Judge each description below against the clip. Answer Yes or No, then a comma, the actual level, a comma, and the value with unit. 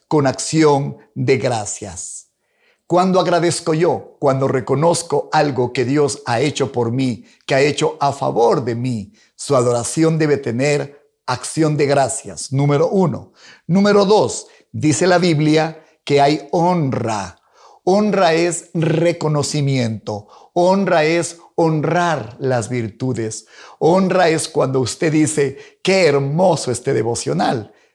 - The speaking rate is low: Yes, slow, 120 wpm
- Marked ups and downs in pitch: No, average, 4.3 semitones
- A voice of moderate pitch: Yes, medium, 145 Hz